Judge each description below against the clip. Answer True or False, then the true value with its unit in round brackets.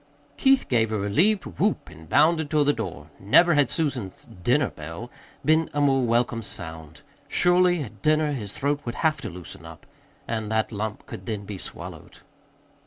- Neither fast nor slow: True (175 wpm)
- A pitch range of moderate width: False (7.0 semitones)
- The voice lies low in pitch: True (120 Hz)